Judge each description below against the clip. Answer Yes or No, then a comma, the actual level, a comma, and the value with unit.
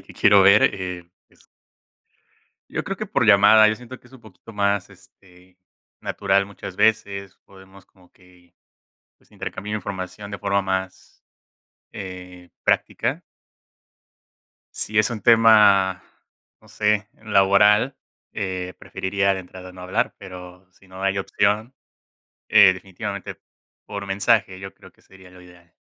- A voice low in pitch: Yes, very low, 95 Hz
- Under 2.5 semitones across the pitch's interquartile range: Yes, narrow, 1.8 semitones